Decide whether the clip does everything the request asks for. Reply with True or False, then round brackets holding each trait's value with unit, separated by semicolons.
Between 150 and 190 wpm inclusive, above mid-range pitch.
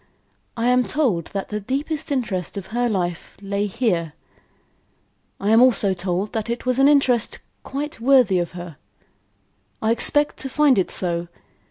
True (160 wpm; 220 Hz)